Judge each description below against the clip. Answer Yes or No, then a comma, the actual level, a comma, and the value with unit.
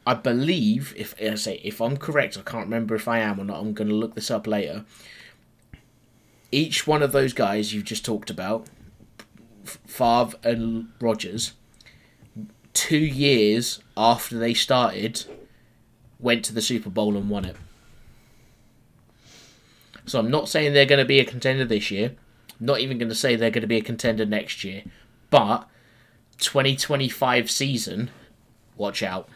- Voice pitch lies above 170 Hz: No, low, 115 Hz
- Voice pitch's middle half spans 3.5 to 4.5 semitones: No, average, 2.7 semitones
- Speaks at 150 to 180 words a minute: Yes, average, 160 wpm